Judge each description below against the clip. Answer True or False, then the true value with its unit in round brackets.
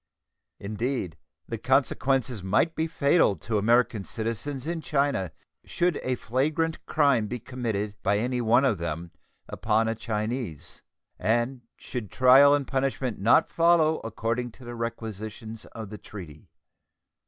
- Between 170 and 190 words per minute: False (135 wpm)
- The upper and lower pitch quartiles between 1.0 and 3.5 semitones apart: False (4.1 semitones)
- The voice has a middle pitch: False (120 Hz)